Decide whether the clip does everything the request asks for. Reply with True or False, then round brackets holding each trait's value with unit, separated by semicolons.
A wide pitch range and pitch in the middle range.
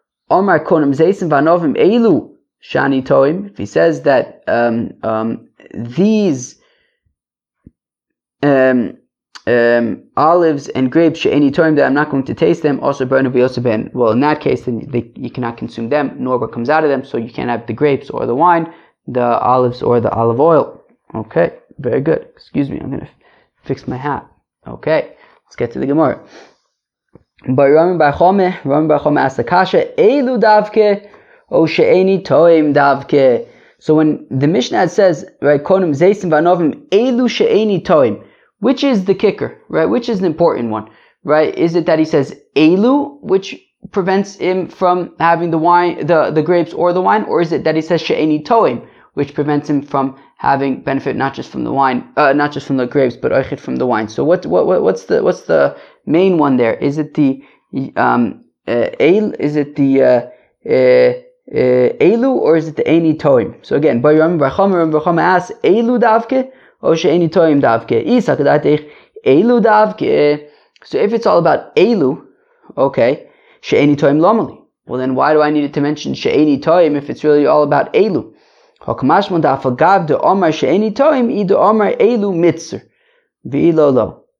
True (6.1 semitones; 155 Hz)